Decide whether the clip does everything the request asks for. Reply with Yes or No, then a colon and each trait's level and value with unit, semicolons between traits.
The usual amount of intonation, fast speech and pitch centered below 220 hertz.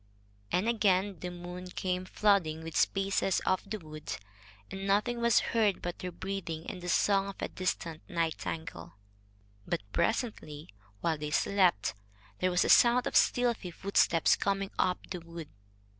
No: average, 3.1 semitones; average, 155 wpm; medium, 185 Hz